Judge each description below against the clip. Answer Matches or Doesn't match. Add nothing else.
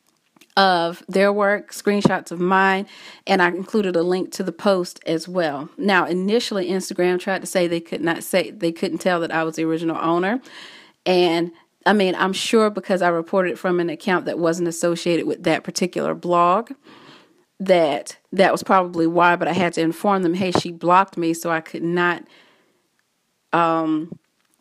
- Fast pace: Doesn't match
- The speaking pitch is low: Doesn't match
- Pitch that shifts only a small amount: Matches